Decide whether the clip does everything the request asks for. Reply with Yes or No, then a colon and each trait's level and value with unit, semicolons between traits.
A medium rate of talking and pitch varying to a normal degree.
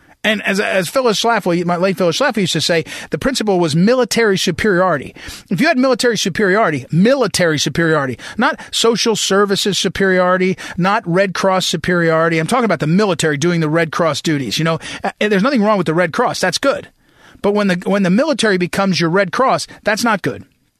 Yes: average, 190 wpm; average, 4.1 semitones